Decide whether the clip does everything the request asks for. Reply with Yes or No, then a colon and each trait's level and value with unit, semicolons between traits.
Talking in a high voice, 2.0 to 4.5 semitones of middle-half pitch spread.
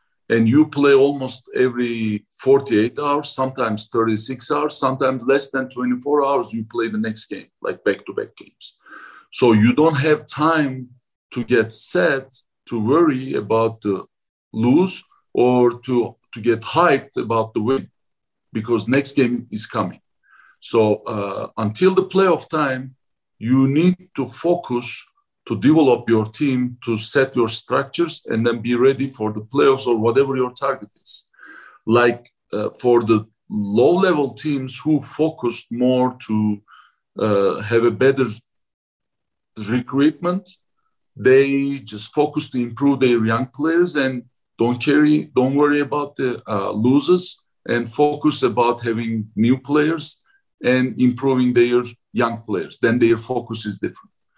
No: low, 125 Hz; average, 3.7 semitones